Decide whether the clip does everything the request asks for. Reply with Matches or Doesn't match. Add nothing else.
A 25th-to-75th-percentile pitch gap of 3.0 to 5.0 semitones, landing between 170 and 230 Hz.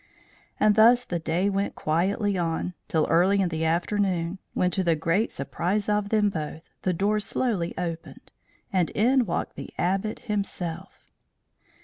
Matches